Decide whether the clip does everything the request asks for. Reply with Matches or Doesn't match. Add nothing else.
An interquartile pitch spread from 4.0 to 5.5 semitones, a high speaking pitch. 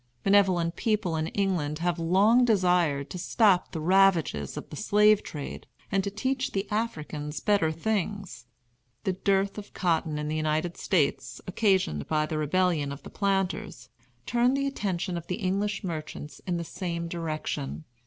Doesn't match